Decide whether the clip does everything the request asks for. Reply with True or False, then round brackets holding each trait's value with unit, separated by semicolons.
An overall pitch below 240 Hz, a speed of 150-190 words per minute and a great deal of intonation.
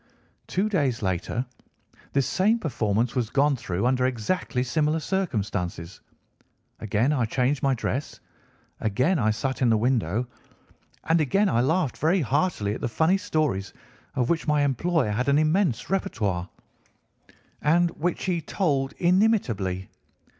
False (135 Hz; 140 wpm; 6.7 semitones)